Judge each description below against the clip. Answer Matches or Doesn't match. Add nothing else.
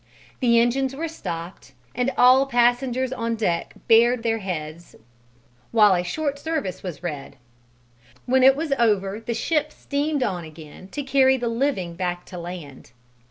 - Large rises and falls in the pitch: Matches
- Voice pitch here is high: Matches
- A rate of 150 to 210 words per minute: Matches